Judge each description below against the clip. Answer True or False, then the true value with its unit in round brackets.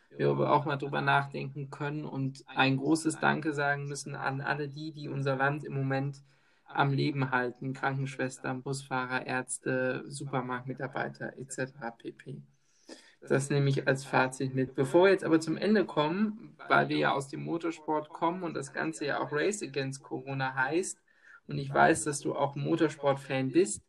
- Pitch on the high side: False (140 Hz)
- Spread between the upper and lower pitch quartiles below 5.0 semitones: True (2.4 semitones)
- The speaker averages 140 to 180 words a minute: True (165 wpm)